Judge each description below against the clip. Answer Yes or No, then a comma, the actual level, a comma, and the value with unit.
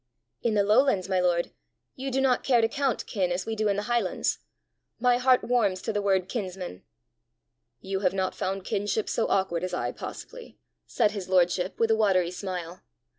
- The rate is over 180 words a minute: Yes, average, 190 wpm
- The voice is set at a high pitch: Yes, high, 200 Hz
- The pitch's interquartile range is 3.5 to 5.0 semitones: Yes, average, 3.9 semitones